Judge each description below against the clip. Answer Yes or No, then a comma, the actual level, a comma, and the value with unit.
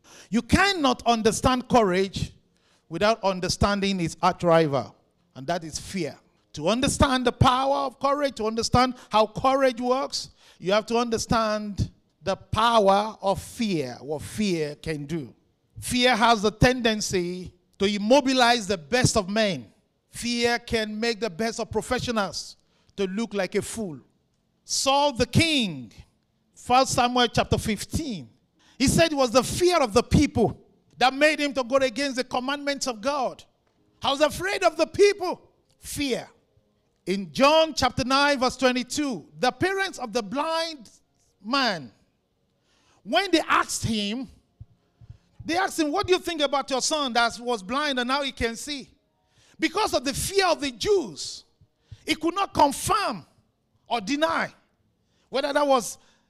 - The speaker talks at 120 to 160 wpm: Yes, average, 150 wpm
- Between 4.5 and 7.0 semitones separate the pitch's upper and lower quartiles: Yes, wide, 5.4 semitones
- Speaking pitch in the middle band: No, high, 245 Hz